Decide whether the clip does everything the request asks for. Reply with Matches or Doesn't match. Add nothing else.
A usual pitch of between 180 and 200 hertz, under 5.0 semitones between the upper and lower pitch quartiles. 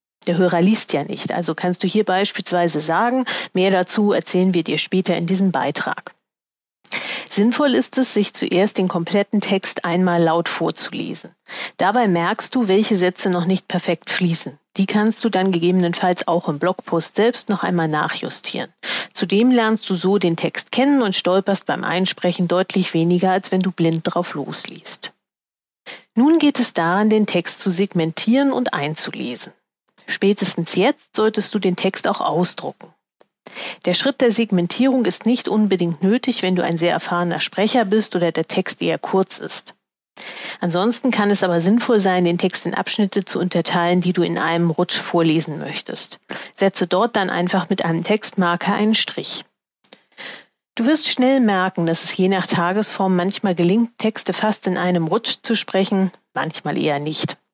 Matches